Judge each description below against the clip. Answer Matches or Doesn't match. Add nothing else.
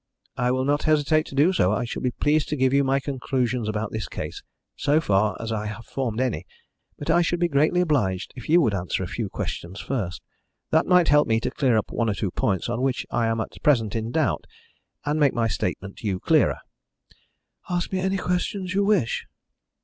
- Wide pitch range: Matches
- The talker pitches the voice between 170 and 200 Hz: Doesn't match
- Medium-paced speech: Doesn't match